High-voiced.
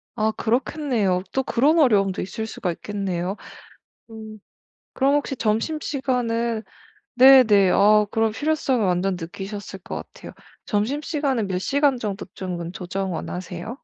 Yes: high, 215 Hz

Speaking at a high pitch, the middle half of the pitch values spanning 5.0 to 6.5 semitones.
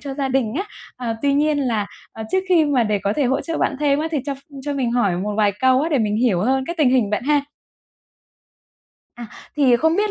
No: very high, 265 Hz; average, 4.4 semitones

